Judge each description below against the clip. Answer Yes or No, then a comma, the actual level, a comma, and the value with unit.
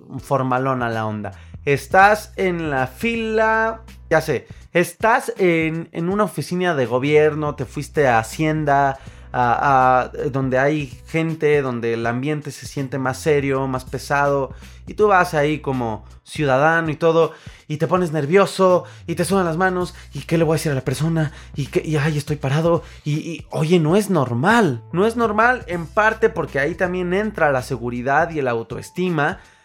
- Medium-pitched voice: Yes, medium, 150 Hz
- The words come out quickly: No, average, 175 wpm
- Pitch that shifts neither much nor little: Yes, average, 4.9 semitones